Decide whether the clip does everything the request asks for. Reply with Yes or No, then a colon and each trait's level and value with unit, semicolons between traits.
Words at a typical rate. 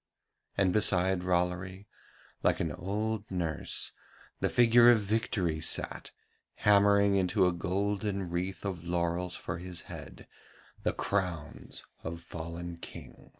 No: slow, 120 wpm